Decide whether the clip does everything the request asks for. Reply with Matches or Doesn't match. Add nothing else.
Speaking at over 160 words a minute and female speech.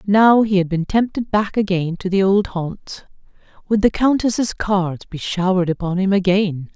Matches